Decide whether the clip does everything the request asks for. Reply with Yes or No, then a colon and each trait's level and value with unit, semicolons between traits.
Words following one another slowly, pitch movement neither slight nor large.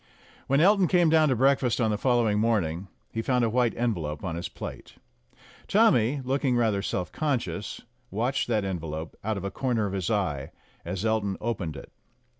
No: average, 185 wpm; average, 5.0 semitones